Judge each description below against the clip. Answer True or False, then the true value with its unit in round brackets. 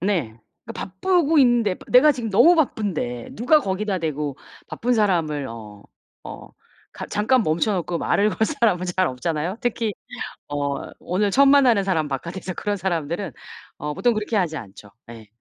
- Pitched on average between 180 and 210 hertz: True (190 Hz)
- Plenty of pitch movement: True (7.0 semitones)